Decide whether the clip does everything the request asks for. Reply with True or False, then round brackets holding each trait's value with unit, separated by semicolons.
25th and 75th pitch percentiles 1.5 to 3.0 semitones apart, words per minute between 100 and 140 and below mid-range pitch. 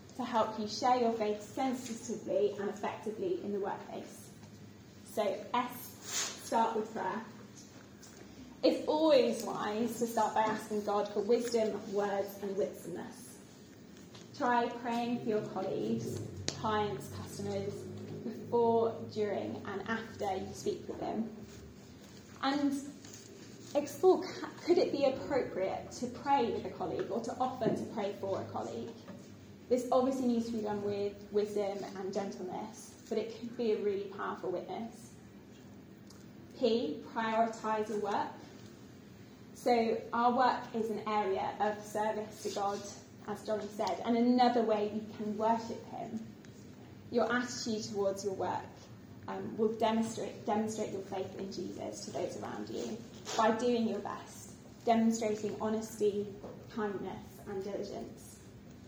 False (2.5 semitones; 135 wpm; 220 Hz)